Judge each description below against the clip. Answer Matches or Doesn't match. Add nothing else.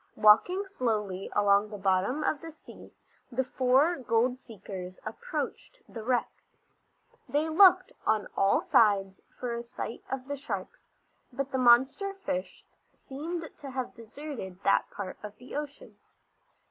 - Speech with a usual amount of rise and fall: Doesn't match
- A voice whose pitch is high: Matches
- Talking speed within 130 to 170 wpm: Matches